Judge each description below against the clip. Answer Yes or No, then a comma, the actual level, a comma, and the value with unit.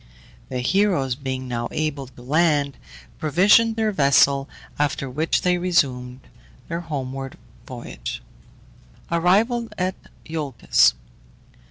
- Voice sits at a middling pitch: Yes, medium, 150 Hz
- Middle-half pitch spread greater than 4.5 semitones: Yes, average, 5.1 semitones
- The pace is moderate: No, slow, 100 wpm